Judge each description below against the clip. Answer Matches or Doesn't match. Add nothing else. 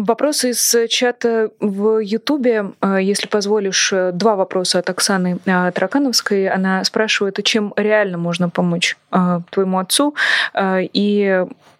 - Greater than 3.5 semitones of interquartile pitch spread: Doesn't match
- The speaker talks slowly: Matches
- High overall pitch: Matches